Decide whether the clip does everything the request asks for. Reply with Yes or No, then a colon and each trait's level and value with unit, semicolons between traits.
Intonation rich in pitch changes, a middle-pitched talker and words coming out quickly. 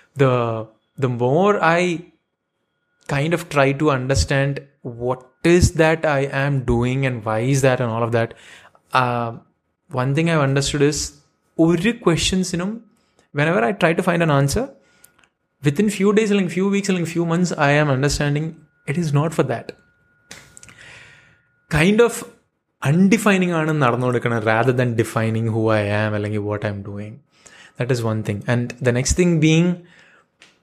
Yes: wide, 5.7 semitones; medium, 145 Hz; fast, 155 wpm